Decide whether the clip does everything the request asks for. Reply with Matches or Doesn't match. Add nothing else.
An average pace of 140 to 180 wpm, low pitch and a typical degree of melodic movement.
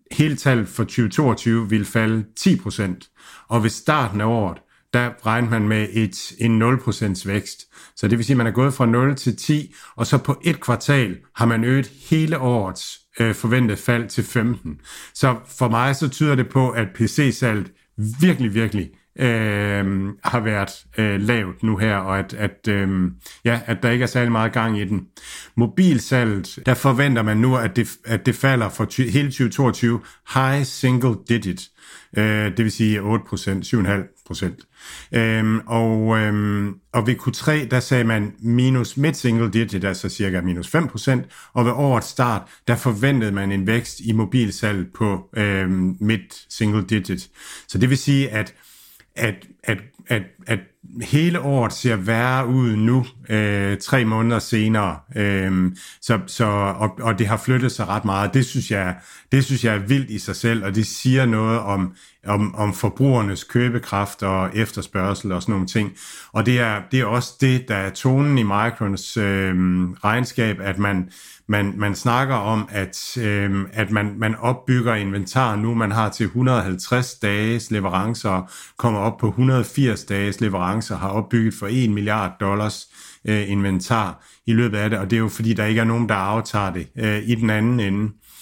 Matches